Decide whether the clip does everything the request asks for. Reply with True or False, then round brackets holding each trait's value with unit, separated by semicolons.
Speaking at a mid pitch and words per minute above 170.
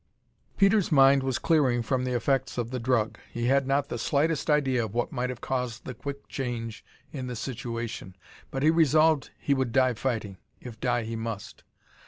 False (125 Hz; 190 wpm)